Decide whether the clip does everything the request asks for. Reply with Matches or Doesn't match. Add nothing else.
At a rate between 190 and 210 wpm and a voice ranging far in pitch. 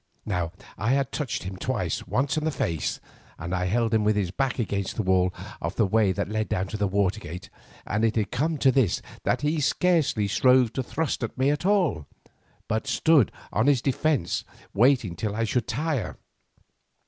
Matches